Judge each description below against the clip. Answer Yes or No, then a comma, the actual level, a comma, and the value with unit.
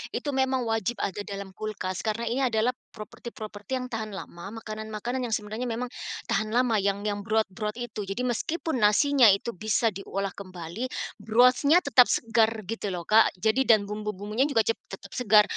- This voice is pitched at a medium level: No, high, 220 Hz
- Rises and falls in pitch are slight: No, average, 3.0 semitones